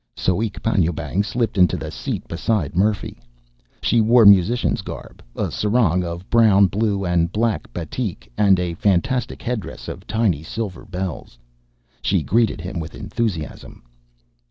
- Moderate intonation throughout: Yes, average, 4.4 semitones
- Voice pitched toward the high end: No, low, 100 Hz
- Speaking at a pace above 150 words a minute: No, slow, 135 wpm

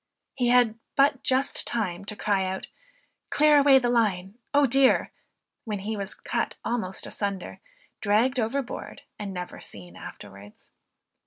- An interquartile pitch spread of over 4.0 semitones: Yes, average, 5.1 semitones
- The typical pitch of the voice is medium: No, high, 220 Hz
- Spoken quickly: No, average, 140 wpm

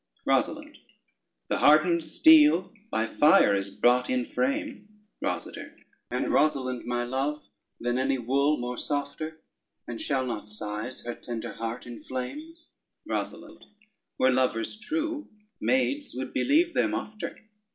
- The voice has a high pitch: No, low, 135 Hz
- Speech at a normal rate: No, slow, 125 wpm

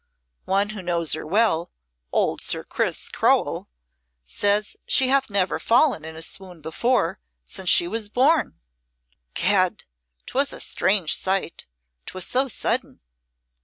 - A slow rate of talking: Yes, slow, 130 wpm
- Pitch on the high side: Yes, high, 195 Hz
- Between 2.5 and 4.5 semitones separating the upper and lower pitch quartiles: No, average, 5.0 semitones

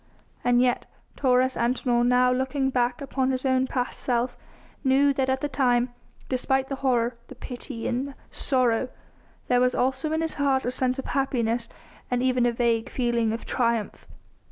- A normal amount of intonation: No, narrow, 1.6 semitones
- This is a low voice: No, very high, 255 Hz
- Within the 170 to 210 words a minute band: Yes, average, 175 wpm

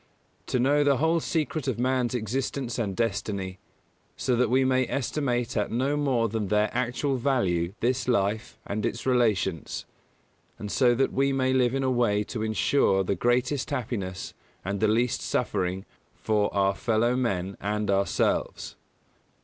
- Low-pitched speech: Yes, low, 120 Hz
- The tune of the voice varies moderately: Yes, average, 4.1 semitones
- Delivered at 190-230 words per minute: No, average, 155 wpm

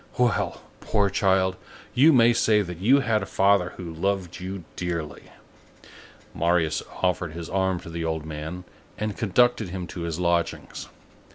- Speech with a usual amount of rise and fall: Yes, average, 3.2 semitones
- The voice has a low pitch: Yes, very low, 90 Hz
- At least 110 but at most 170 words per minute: Yes, average, 155 wpm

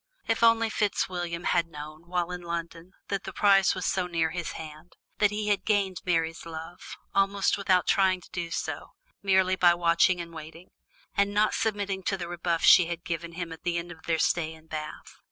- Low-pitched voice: No, medium, 175 Hz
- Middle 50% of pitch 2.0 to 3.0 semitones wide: Yes, narrow, 2.6 semitones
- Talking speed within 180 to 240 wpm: Yes, average, 200 wpm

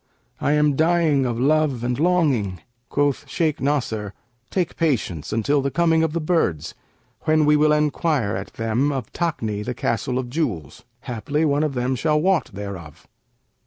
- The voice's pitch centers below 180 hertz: Yes, medium, 140 Hz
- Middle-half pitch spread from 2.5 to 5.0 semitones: No, wide, 5.4 semitones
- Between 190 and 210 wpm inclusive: No, average, 160 wpm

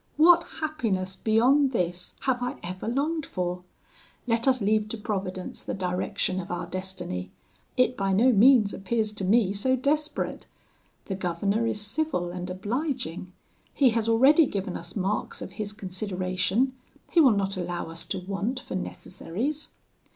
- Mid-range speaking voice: No, high, 210 Hz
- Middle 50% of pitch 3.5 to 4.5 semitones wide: No, wide, 5.4 semitones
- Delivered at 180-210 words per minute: No, average, 155 wpm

